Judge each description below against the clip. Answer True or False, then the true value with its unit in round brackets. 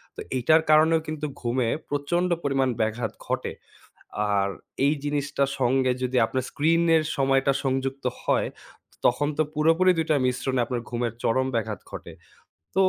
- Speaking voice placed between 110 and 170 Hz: True (135 Hz)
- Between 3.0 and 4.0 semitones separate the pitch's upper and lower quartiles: True (3.6 semitones)